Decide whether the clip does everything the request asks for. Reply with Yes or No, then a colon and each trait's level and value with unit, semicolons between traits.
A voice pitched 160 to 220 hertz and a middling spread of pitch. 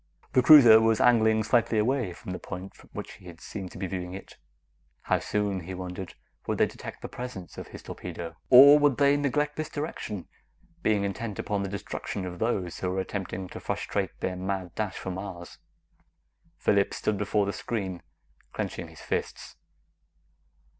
No: low, 100 Hz; average, 4.0 semitones